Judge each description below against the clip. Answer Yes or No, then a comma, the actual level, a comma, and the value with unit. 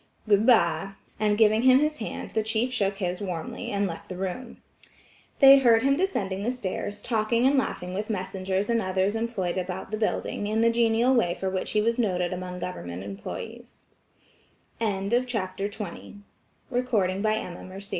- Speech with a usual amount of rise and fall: Yes, average, 3.8 semitones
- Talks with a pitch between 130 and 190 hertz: No, high, 210 Hz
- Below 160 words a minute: Yes, average, 150 wpm